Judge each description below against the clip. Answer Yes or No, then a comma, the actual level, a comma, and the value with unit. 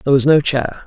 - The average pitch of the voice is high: No, medium, 140 Hz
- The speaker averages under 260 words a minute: No, fast, 280 wpm